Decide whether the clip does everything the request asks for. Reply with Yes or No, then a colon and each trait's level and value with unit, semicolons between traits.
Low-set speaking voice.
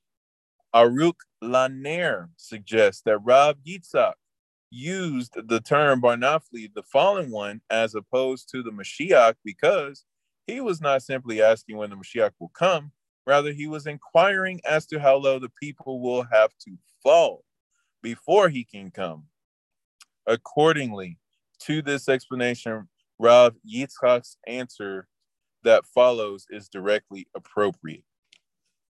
Yes: low, 125 Hz